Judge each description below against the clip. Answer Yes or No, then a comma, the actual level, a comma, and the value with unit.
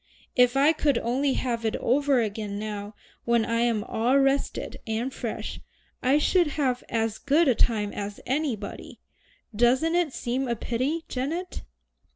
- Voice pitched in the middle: No, very high, 250 Hz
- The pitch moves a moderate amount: Yes, average, 3.9 semitones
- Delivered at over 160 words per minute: No, average, 155 wpm